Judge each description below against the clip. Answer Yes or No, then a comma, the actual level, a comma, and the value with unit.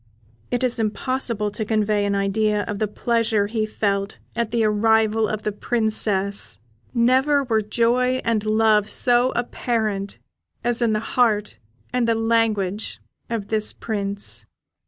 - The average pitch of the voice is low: No, high, 220 Hz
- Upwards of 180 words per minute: No, slow, 135 wpm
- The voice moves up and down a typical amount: No, narrow, 2.1 semitones